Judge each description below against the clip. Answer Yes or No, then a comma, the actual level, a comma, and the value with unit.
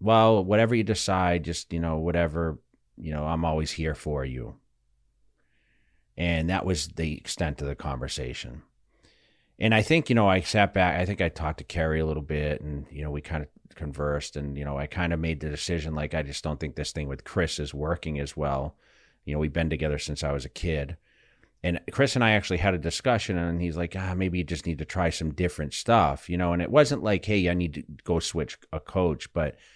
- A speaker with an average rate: No, fast, 230 wpm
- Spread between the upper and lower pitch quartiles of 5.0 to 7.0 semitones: No, average, 3.2 semitones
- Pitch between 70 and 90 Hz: Yes, very low, 80 Hz